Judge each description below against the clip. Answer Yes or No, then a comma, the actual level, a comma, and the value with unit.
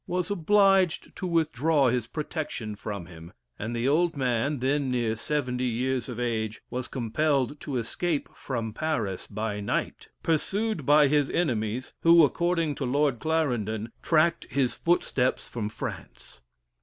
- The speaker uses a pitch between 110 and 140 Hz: Yes, low, 135 Hz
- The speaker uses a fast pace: No, average, 145 wpm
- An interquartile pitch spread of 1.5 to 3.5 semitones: No, average, 5.3 semitones